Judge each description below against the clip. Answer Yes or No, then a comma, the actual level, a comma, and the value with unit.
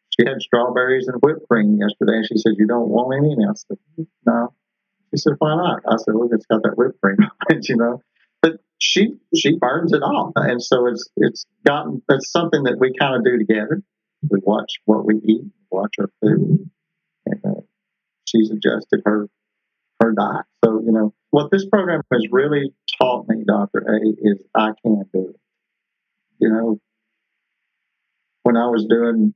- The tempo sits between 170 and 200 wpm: Yes, average, 180 wpm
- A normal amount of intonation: No, wide, 6.0 semitones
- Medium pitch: No, low, 120 Hz